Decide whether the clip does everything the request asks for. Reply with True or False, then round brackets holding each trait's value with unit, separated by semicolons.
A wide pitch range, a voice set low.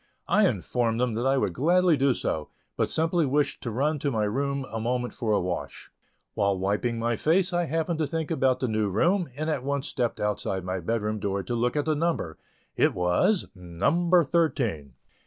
True (6.9 semitones; 125 Hz)